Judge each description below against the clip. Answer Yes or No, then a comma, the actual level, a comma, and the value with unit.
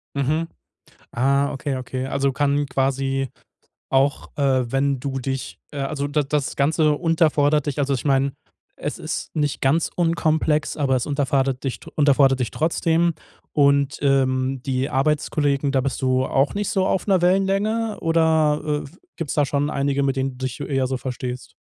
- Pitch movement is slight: Yes, narrow, 2.3 semitones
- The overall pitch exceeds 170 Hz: No, medium, 140 Hz